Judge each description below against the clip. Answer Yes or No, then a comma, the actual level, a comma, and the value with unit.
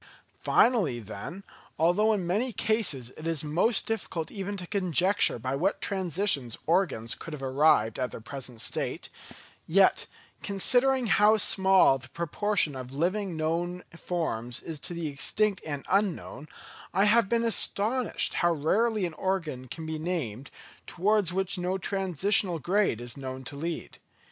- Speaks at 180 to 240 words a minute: No, average, 150 wpm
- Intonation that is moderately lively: No, wide, 5.8 semitones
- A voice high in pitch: No, medium, 175 Hz